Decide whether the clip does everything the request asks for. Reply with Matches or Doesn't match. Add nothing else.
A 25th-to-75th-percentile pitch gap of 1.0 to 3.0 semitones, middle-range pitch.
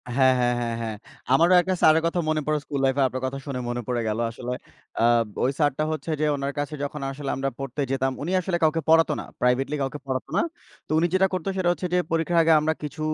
Doesn't match